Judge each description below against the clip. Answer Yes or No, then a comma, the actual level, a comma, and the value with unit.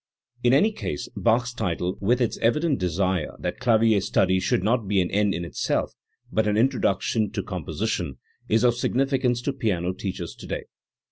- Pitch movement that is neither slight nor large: Yes, average, 4.7 semitones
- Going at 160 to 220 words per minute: Yes, average, 175 wpm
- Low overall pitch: Yes, low, 110 Hz